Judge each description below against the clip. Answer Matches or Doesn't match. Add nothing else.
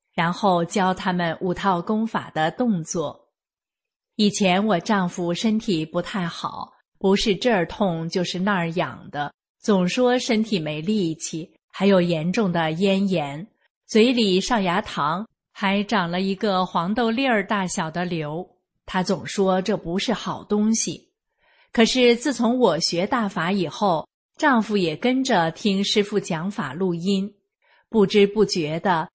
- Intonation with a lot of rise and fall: Doesn't match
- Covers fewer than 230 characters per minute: Matches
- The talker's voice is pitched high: Matches